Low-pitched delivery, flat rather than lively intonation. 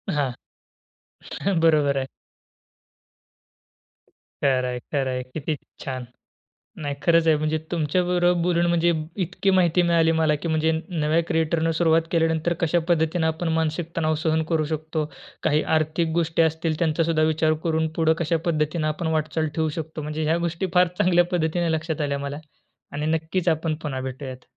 No: medium, 160 Hz; narrow, 1.6 semitones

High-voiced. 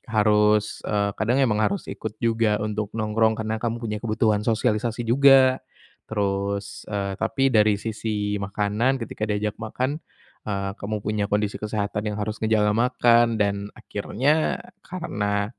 No: low, 110 Hz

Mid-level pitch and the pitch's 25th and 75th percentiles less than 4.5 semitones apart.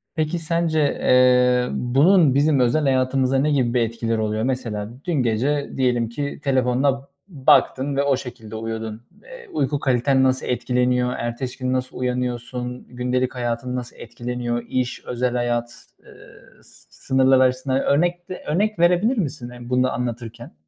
No: low, 125 Hz; narrow, 2.4 semitones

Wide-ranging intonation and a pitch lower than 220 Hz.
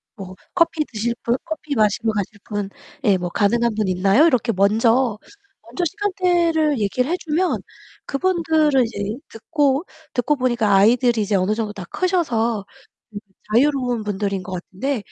No: wide, 6.4 semitones; high, 235 Hz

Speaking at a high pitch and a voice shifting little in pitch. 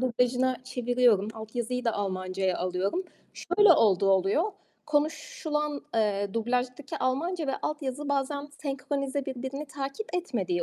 No: very high, 255 Hz; average, 5.0 semitones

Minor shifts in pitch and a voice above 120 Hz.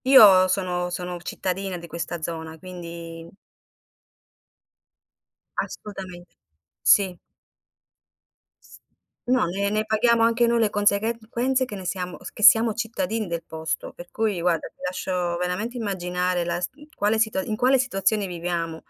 No: average, 3.9 semitones; high, 190 Hz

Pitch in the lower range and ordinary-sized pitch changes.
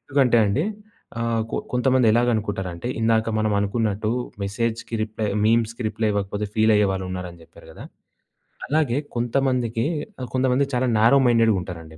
Yes: low, 115 Hz; average, 3.1 semitones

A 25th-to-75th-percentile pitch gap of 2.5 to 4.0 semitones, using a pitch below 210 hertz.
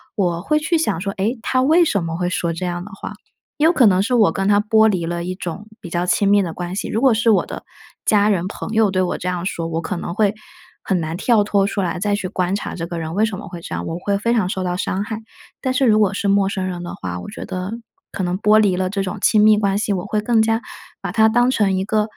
Yes: average, 3.3 semitones; high, 200 Hz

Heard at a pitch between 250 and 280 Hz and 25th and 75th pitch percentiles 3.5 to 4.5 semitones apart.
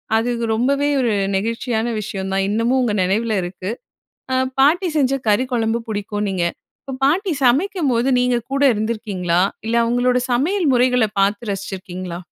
No: high, 230 Hz; average, 4.1 semitones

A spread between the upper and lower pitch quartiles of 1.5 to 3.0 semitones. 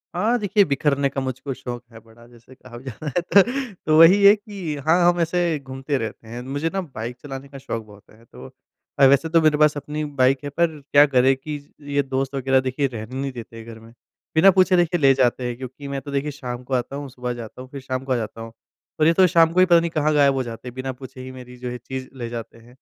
No: average, 3.7 semitones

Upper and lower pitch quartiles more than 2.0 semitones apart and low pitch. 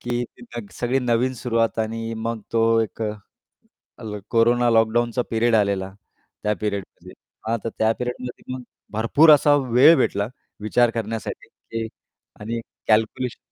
No: narrow, 1.7 semitones; low, 115 Hz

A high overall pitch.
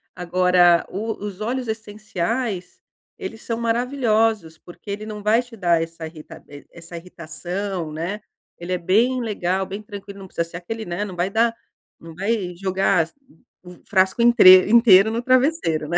Yes: high, 195 Hz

